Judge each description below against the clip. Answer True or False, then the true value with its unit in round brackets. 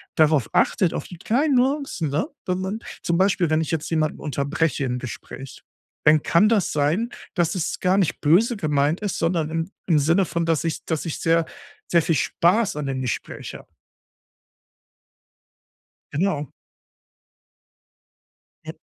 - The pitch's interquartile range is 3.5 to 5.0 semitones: True (4.1 semitones)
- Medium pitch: True (165 Hz)